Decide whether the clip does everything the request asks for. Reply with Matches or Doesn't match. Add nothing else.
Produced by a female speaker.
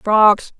Matches